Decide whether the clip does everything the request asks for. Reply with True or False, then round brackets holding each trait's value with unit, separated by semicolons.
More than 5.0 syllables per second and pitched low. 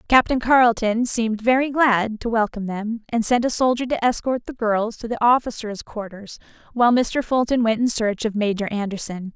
False (5.3 syllables/s; 225 Hz)